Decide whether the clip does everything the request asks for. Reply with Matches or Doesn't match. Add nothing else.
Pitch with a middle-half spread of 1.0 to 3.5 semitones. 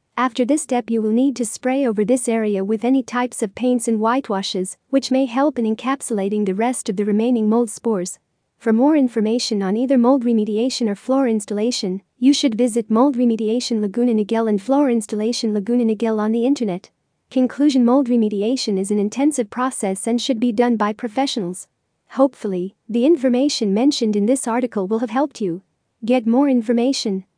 Matches